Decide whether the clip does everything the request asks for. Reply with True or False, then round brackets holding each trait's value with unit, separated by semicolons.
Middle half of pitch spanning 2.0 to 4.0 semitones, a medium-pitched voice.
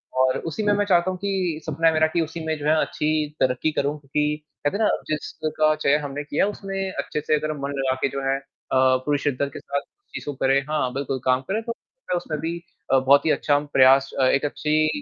True (2.7 semitones; 150 Hz)